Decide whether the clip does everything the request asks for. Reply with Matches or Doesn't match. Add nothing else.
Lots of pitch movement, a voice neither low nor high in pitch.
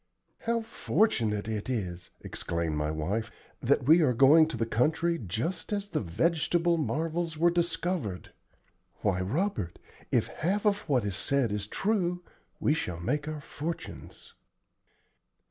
Matches